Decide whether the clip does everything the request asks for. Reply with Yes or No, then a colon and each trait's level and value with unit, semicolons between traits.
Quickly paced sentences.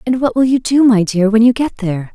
Yes: fast, 305 wpm